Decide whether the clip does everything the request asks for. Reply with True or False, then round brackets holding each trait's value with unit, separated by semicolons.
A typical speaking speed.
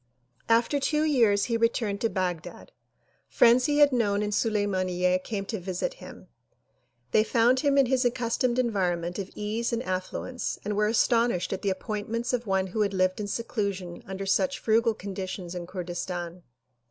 True (165 wpm)